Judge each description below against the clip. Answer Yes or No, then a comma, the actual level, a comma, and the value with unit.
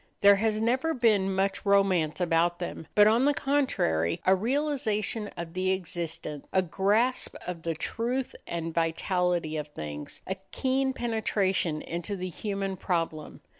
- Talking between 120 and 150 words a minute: Yes, average, 145 wpm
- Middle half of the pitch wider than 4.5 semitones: Yes, average, 4.9 semitones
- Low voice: No, high, 190 Hz